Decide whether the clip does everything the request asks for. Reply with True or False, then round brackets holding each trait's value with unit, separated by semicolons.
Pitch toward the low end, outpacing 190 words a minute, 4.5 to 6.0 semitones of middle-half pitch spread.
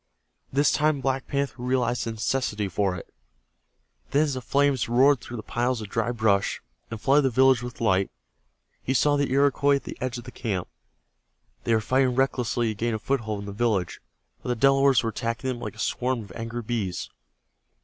False (120 Hz; 200 wpm; 3.2 semitones)